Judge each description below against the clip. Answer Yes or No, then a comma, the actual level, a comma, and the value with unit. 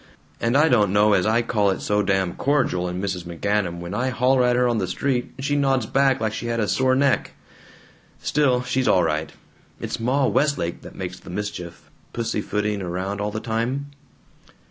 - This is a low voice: Yes, low, 110 Hz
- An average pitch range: Yes, average, 5.0 semitones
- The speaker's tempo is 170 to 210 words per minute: Yes, average, 195 wpm